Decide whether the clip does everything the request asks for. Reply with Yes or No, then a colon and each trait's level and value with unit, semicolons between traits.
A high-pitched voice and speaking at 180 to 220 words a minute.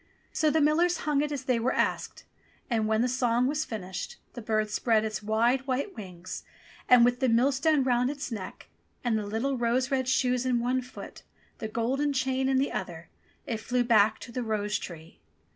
Yes: high, 245 Hz; average, 195 wpm